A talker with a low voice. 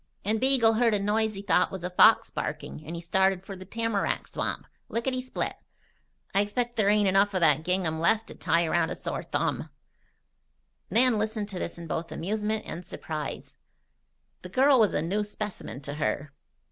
No: high, 200 Hz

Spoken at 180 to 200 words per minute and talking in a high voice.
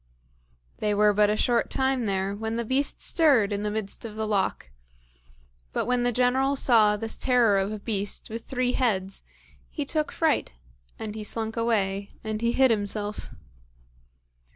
No: average, 170 wpm; high, 220 Hz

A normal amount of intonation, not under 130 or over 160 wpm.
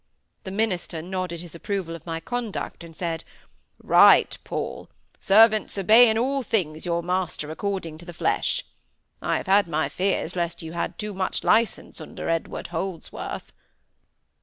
Yes: average, 3.7 semitones; average, 150 wpm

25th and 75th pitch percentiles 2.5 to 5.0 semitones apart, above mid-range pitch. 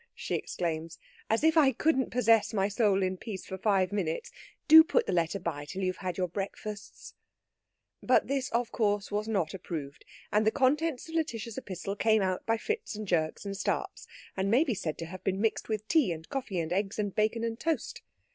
Yes: average, 4.1 semitones; high, 205 Hz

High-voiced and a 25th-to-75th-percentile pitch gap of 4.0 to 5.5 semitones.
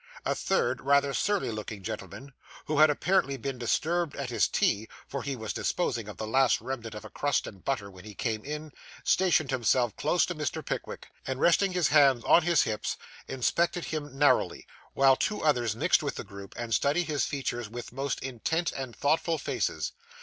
No: low, 135 Hz; average, 4.6 semitones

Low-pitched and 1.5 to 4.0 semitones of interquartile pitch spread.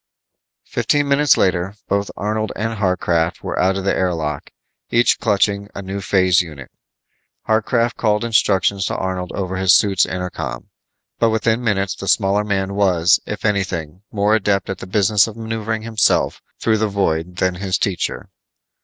Yes: low, 100 Hz; average, 2.8 semitones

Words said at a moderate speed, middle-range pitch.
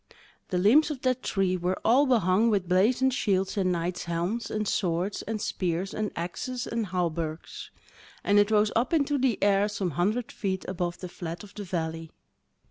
No: average, 180 wpm; high, 195 Hz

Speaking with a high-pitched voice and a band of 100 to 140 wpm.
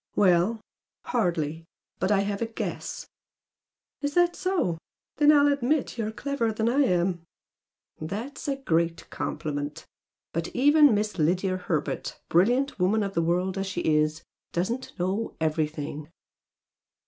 Yes: high, 195 Hz; slow, 135 wpm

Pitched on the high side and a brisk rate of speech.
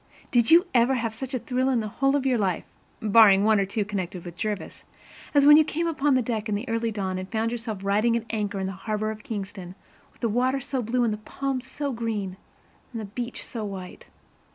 Yes: high, 225 Hz; fast, 235 wpm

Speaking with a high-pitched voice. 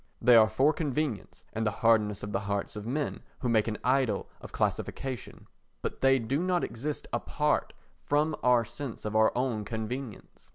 No: low, 120 Hz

